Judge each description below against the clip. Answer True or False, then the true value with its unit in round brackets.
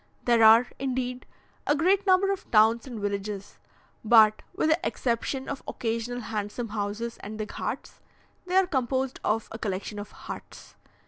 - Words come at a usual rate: True (155 wpm)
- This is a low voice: False (235 Hz)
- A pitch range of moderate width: True (3.8 semitones)